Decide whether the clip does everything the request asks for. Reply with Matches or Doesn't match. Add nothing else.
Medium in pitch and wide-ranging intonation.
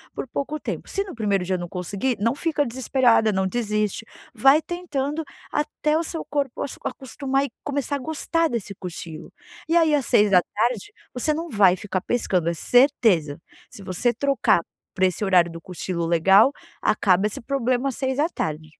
Doesn't match